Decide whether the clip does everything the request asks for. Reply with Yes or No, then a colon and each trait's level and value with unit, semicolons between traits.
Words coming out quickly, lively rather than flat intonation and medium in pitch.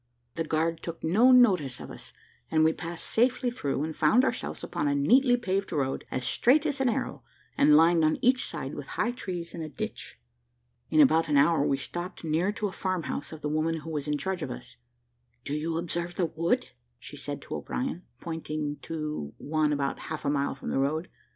No: fast, 210 wpm; average, 4.1 semitones; medium, 165 Hz